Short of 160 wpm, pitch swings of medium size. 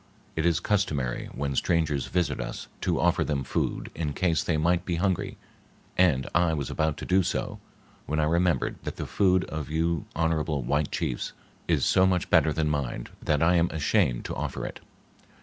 No: average, 185 wpm; average, 3.2 semitones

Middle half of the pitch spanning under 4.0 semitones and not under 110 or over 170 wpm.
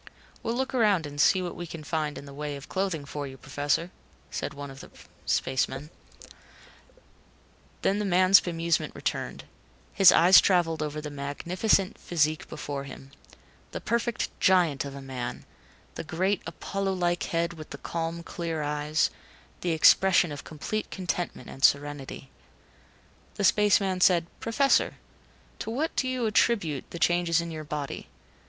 No: average, 4.4 semitones; average, 155 wpm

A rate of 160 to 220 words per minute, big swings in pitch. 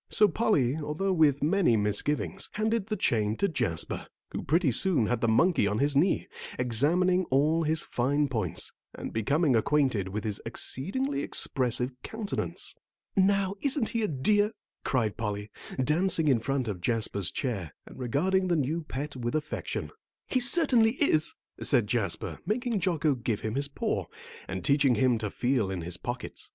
Yes: average, 165 wpm; wide, 8.3 semitones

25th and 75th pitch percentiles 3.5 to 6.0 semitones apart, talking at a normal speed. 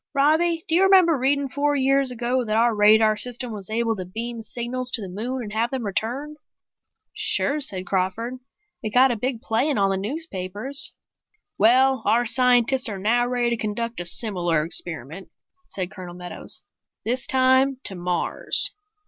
Yes: average, 4.2 semitones; average, 170 wpm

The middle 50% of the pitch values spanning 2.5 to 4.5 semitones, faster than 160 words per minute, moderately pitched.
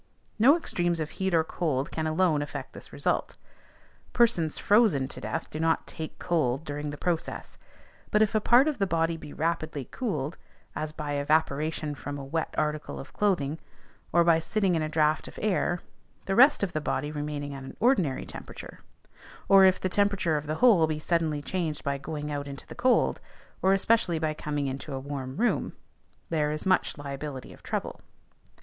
Yes: average, 4.2 semitones; average, 185 wpm; medium, 155 Hz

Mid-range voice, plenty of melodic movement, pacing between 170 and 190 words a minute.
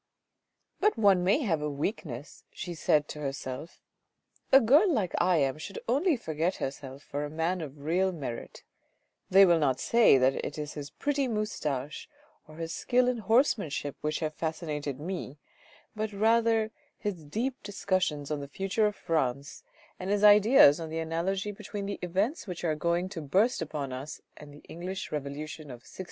Yes: medium, 170 Hz; wide, 5.8 semitones; average, 180 wpm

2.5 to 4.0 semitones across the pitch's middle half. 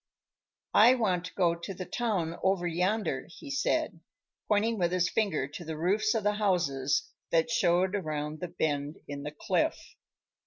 No: average, 4.6 semitones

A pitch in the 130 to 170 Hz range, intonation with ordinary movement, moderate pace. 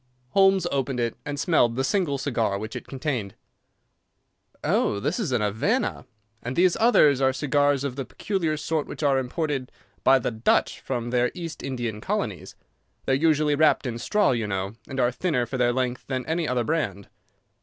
Yes: low, 135 Hz; average, 4.1 semitones; average, 185 wpm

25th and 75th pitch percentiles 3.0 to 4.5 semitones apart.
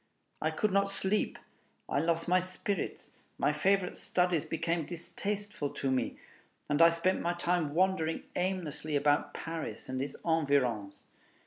Yes: average, 4.1 semitones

